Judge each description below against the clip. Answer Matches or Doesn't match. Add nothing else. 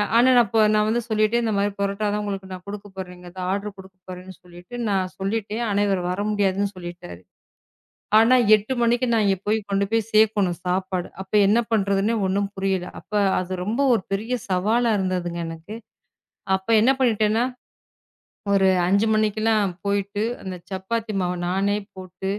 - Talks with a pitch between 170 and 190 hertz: Doesn't match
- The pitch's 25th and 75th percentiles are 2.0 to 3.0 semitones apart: Matches